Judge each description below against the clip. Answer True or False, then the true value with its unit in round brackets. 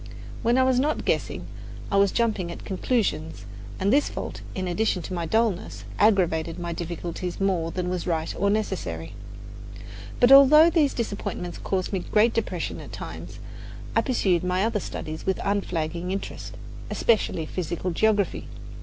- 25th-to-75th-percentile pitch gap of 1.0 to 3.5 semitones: False (4.3 semitones)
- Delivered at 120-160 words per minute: True (155 wpm)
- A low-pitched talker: False (190 Hz)